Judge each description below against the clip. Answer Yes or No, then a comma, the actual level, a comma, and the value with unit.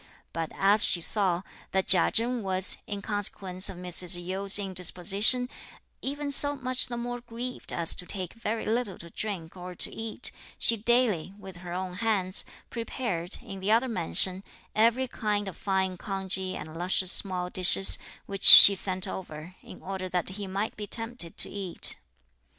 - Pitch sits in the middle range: No, high, 195 Hz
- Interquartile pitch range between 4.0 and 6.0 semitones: No, average, 3.6 semitones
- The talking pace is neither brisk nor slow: Yes, average, 165 wpm